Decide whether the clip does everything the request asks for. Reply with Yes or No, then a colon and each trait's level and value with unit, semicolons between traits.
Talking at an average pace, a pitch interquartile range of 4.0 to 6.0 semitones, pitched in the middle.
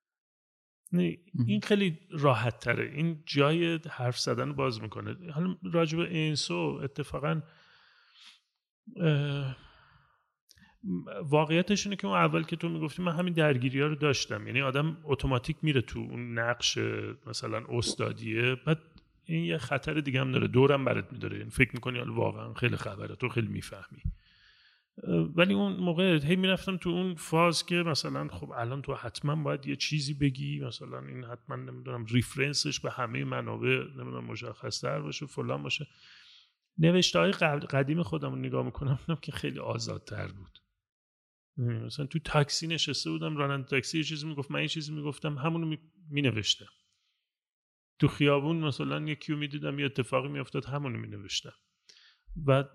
Yes: average, 145 wpm; average, 4.8 semitones; medium, 145 Hz